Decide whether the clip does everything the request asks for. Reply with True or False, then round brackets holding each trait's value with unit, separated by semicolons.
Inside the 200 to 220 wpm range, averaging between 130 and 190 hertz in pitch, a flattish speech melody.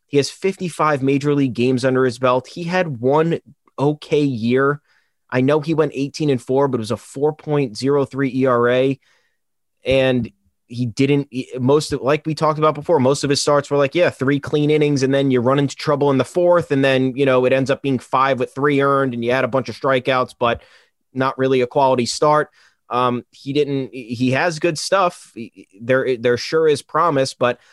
True (205 wpm; 135 Hz; 2.3 semitones)